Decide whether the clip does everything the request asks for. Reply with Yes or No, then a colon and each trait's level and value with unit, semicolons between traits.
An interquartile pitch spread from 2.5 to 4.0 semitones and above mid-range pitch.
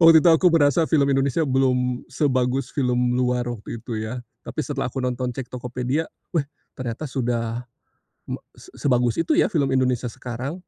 No: average, 2.9 semitones; low, 130 Hz